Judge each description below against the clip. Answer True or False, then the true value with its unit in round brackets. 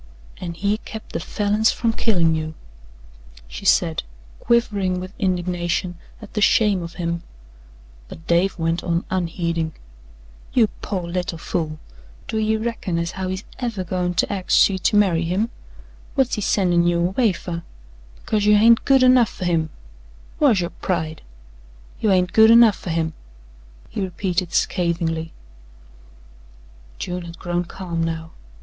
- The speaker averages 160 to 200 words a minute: False (150 wpm)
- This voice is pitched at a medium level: True (180 Hz)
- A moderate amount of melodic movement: True (3.6 semitones)